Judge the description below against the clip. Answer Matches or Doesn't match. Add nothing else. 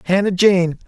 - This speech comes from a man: Matches